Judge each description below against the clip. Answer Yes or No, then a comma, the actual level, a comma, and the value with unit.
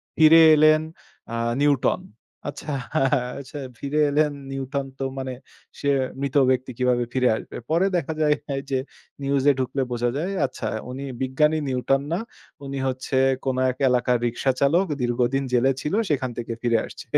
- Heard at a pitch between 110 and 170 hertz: Yes, low, 135 Hz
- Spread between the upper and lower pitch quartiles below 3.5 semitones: Yes, narrow, 2.6 semitones